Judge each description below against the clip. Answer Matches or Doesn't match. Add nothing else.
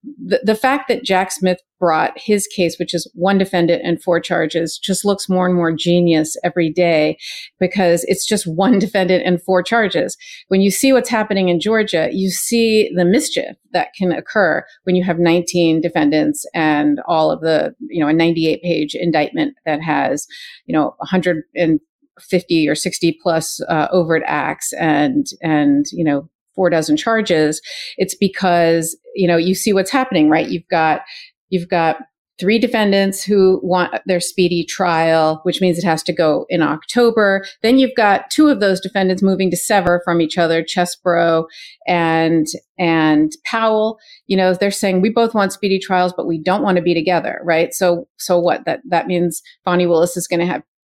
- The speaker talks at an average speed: Matches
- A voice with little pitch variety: Doesn't match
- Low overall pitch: Doesn't match